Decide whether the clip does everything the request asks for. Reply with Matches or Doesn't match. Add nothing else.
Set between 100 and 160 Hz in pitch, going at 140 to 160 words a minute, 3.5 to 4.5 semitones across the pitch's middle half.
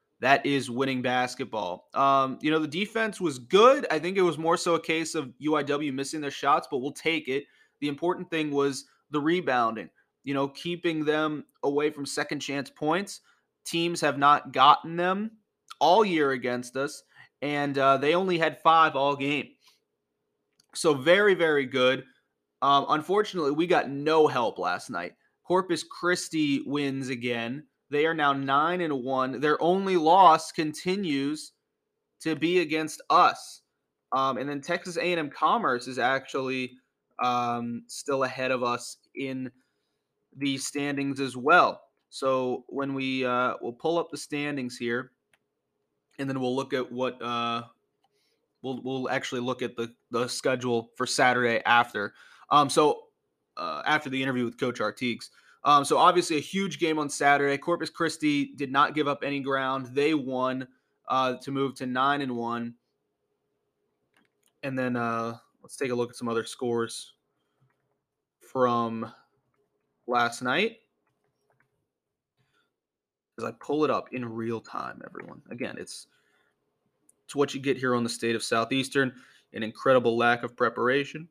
Matches